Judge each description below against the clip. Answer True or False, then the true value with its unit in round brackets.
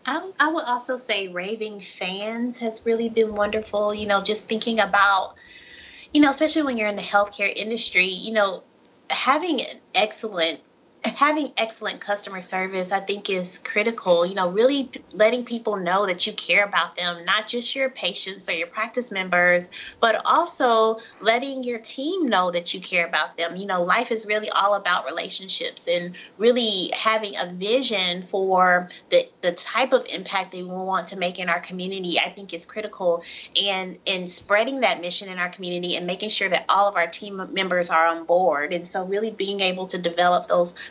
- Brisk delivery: False (190 wpm)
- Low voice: False (200 Hz)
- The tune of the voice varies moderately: True (3.8 semitones)